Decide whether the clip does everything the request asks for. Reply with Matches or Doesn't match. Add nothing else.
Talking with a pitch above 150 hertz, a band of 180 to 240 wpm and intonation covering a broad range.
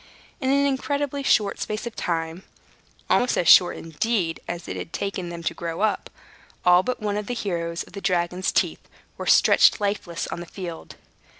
Doesn't match